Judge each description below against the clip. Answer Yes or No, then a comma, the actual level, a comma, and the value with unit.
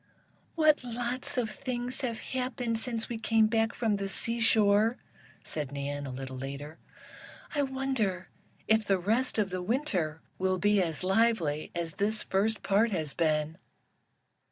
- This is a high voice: Yes, high, 215 Hz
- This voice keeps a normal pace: Yes, average, 145 wpm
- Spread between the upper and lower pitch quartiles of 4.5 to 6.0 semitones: Yes, wide, 5.5 semitones